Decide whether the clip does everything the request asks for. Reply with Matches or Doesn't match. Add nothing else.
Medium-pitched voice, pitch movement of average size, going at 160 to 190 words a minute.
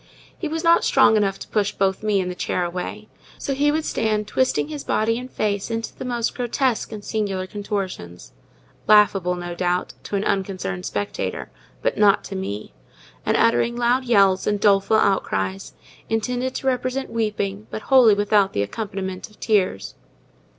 Doesn't match